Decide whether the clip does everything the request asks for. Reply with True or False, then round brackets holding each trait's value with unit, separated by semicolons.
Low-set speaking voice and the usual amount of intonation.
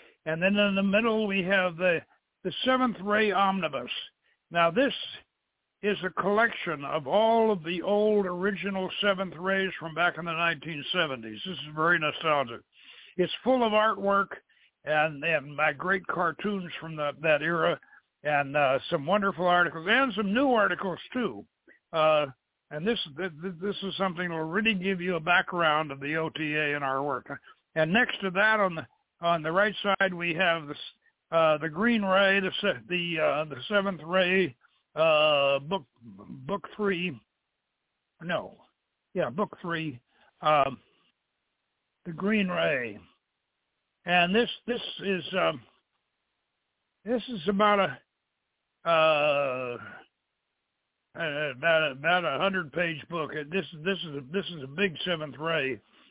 False (180 Hz; 4.3 semitones)